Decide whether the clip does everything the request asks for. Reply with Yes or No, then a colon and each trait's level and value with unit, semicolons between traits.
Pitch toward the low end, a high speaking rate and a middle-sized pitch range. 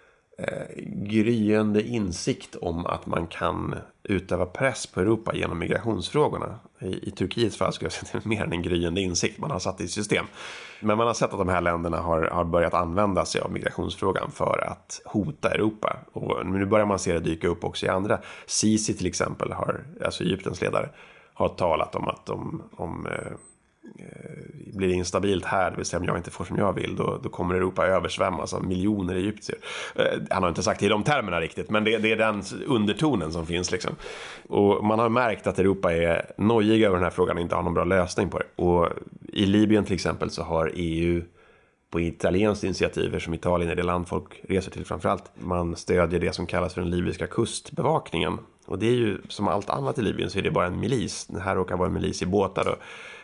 Yes: very low, 95 Hz; fast, 220 wpm; average, 3.5 semitones